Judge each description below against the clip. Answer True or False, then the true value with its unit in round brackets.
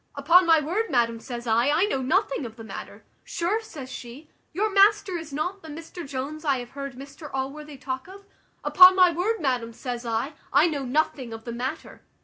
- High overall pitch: True (285 Hz)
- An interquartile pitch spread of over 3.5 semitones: True (5.1 semitones)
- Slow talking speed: False (200 wpm)